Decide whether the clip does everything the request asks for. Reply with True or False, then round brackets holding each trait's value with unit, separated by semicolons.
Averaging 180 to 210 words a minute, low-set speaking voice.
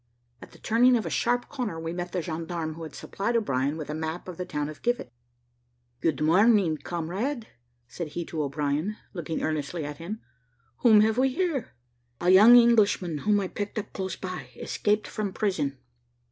False (185 wpm; 180 Hz)